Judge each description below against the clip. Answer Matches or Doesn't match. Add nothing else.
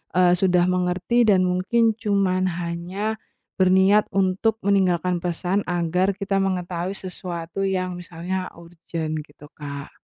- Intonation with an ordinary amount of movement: Doesn't match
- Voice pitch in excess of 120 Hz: Matches